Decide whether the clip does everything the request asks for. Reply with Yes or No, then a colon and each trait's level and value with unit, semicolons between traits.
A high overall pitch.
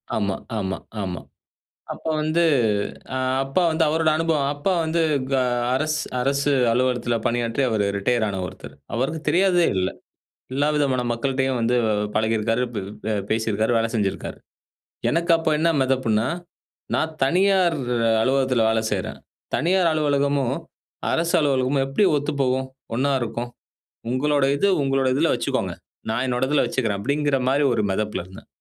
No: low, 135 Hz